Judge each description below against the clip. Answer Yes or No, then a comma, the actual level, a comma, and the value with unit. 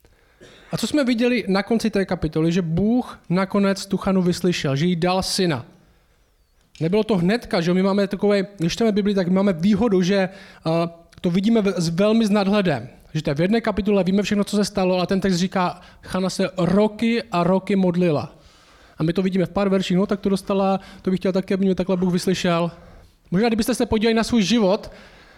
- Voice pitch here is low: No, high, 190 Hz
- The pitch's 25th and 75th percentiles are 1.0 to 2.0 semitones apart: No, narrow, 2.5 semitones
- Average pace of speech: No, fast, 200 wpm